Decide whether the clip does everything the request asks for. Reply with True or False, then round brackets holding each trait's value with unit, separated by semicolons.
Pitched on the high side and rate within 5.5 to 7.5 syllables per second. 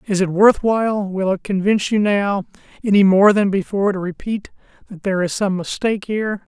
True (200 Hz; 5.7 syllables/s)